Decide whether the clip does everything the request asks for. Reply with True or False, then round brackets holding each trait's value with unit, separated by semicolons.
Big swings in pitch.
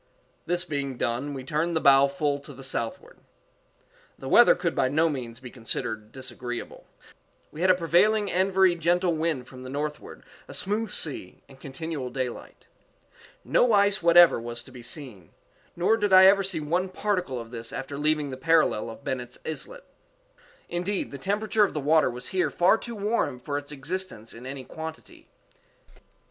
True (6.1 semitones)